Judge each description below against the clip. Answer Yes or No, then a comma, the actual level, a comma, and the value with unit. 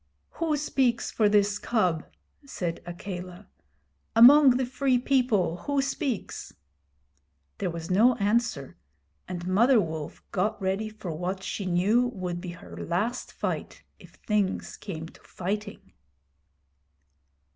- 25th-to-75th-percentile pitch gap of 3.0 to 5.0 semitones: No, wide, 5.4 semitones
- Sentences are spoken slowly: Yes, slow, 125 wpm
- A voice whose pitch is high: Yes, high, 205 Hz